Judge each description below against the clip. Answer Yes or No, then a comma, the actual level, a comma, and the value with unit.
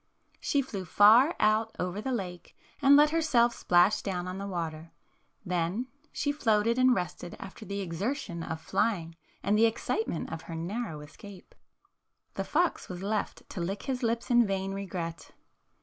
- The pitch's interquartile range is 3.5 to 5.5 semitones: Yes, average, 5.1 semitones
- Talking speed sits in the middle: Yes, average, 165 wpm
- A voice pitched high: Yes, high, 200 Hz